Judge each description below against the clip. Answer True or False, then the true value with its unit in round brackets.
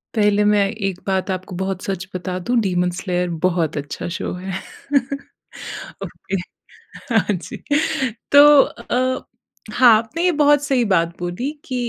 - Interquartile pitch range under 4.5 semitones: False (5.1 semitones)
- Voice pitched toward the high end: True (195 Hz)